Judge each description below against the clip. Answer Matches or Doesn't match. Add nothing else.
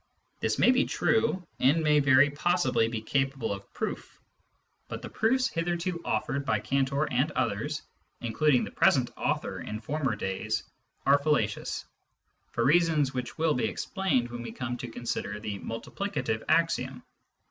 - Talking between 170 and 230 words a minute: Doesn't match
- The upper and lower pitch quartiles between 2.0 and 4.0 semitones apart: Doesn't match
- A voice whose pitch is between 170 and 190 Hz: Doesn't match